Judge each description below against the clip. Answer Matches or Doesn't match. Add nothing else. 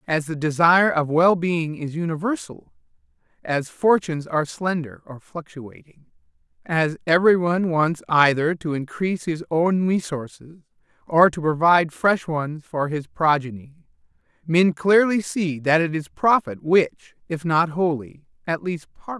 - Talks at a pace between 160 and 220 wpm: Doesn't match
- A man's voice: Matches